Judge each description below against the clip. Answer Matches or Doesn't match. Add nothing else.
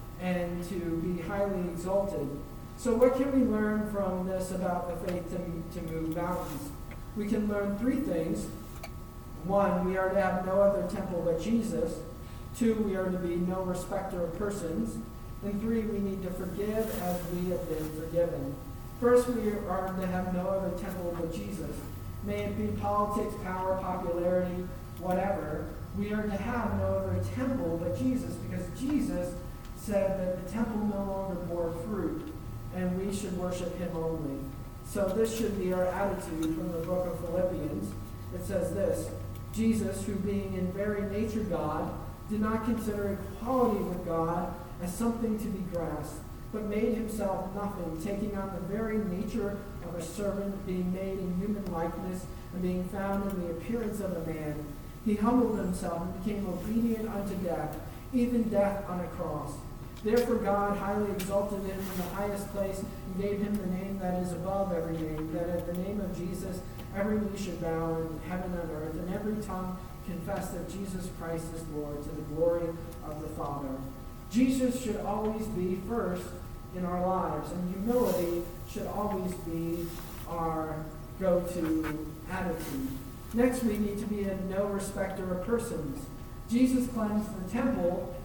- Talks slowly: Doesn't match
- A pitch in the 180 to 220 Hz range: Matches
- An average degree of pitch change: Matches